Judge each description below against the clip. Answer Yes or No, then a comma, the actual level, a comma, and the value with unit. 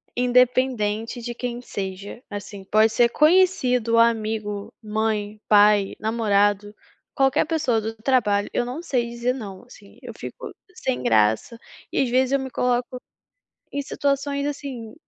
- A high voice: Yes, high, 235 Hz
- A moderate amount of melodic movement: Yes, average, 3.5 semitones